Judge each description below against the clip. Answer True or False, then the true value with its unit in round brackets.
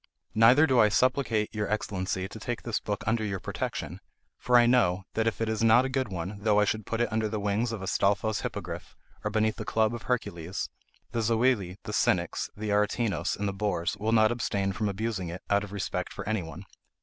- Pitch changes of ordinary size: False (2.3 semitones)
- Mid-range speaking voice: False (110 Hz)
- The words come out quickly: True (215 wpm)